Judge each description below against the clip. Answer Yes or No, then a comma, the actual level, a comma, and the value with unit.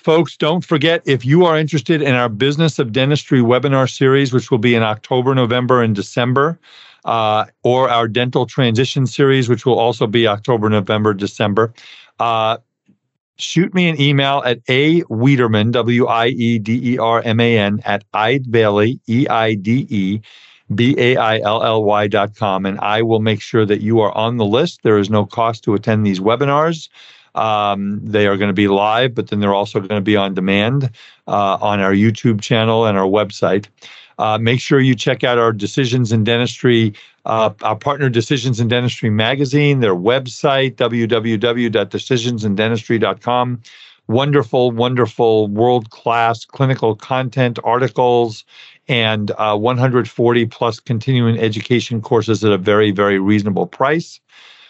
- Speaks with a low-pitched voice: Yes, low, 115 Hz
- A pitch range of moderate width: Yes, average, 3.1 semitones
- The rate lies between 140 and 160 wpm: Yes, average, 145 wpm